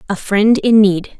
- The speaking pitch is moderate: No, high, 205 Hz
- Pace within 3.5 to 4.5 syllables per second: Yes, 4.0 syllables/s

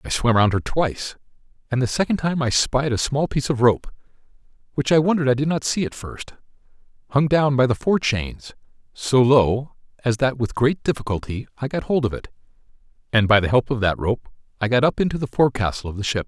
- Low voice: Yes, low, 125 Hz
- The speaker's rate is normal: No, fast, 220 wpm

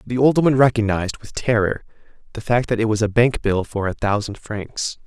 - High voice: No, low, 110 Hz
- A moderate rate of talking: No, fast, 215 wpm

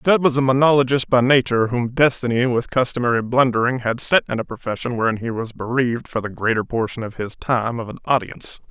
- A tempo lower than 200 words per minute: No, fast, 205 wpm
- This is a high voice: No, low, 120 Hz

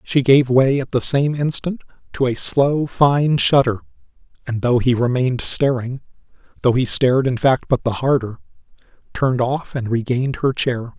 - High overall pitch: No, low, 130 Hz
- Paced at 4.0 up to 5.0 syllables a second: Yes, 4.8 syllables/s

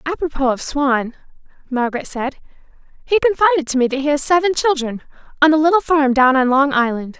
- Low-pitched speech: No, very high, 285 Hz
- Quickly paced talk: No, average, 175 wpm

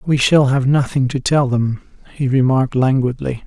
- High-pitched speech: No, low, 130 Hz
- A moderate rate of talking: Yes, average, 175 wpm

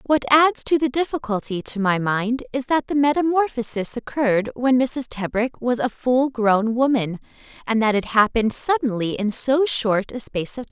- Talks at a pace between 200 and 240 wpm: No, average, 185 wpm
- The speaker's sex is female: Yes, female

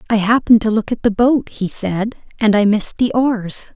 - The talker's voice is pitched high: Yes, high, 220 Hz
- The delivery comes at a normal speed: No, fast, 225 wpm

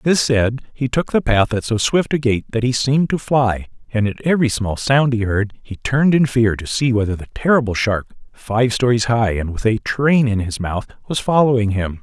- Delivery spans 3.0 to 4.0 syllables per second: No, 5.1 syllables/s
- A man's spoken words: Yes, male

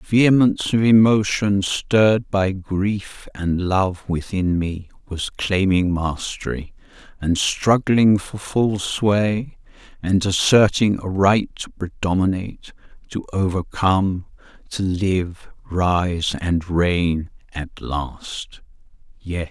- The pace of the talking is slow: Yes, slow, 115 wpm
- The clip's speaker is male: Yes, male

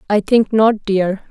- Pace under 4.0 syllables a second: Yes, 3.7 syllables/s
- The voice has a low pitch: No, high, 210 Hz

